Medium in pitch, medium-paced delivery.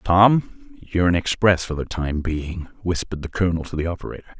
No: very low, 85 Hz; average, 190 wpm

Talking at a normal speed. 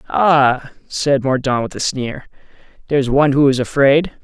Yes: average, 155 wpm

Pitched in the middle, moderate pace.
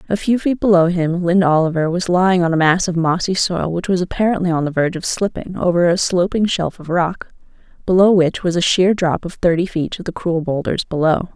No: medium, 175 Hz; fast, 225 wpm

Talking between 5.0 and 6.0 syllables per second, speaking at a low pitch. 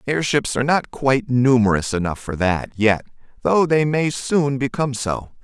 No: 4.8 syllables/s; low, 130 Hz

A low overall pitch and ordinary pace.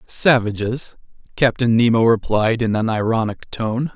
No: low, 115 Hz; slow, 120 wpm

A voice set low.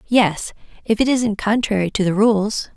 No: high, 210 Hz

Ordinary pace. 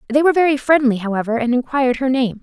No: fast, 225 wpm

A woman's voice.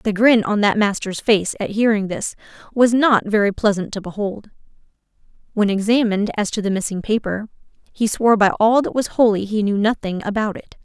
Yes: female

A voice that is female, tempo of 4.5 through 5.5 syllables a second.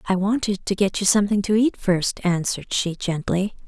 Yes: female; 5.3 syllables/s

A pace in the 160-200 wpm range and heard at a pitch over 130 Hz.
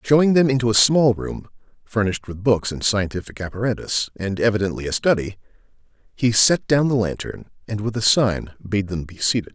No: average, 180 wpm; low, 110 Hz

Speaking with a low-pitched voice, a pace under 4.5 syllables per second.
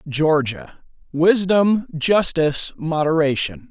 No: medium, 165 Hz; 3.5 syllables/s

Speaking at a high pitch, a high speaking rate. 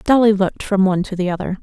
Yes: high, 195 Hz; fast, 260 wpm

